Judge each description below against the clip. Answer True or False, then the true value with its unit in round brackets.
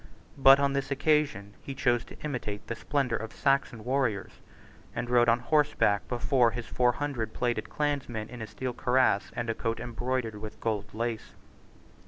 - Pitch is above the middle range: False (120 Hz)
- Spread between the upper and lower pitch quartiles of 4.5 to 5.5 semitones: False (3.3 semitones)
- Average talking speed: True (170 wpm)